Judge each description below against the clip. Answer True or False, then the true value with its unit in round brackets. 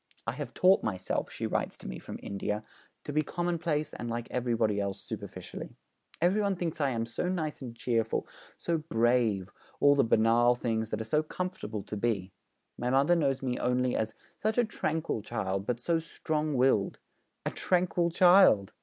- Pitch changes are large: True (6.6 semitones)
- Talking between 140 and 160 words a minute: False (180 wpm)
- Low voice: True (125 Hz)